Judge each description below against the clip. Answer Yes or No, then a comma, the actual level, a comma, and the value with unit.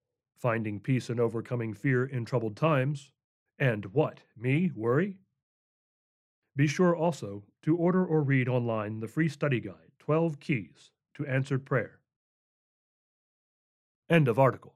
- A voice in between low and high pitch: No, low, 130 Hz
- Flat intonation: No, average, 5.1 semitones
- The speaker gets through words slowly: Yes, slow, 130 wpm